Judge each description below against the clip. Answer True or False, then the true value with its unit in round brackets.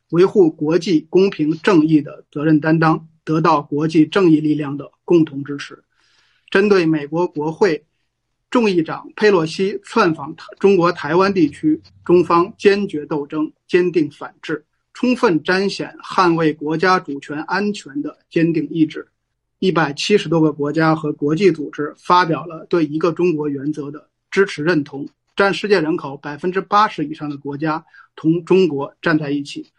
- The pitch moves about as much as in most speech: True (3.8 semitones)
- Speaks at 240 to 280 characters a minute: True (250 characters per minute)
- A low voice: False (160 Hz)